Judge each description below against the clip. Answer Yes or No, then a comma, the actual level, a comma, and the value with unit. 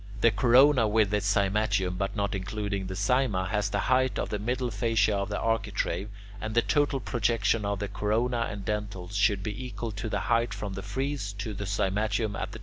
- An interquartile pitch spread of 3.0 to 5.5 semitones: No, narrow, 2.5 semitones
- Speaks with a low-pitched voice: Yes, low, 105 Hz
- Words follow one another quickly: Yes, fast, 225 wpm